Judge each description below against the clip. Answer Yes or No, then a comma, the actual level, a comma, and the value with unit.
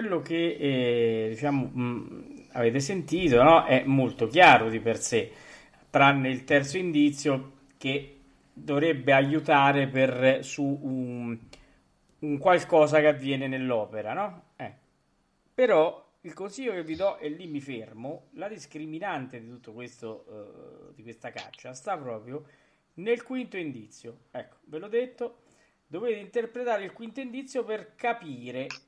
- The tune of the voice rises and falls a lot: Yes, wide, 6.1 semitones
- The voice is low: No, medium, 145 Hz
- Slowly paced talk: No, average, 135 wpm